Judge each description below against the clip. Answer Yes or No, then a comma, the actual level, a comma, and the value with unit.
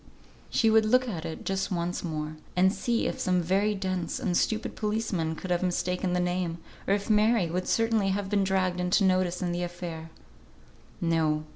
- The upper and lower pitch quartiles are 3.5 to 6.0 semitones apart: No, average, 2.7 semitones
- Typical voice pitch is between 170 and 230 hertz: Yes, medium, 185 Hz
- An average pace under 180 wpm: No, average, 185 wpm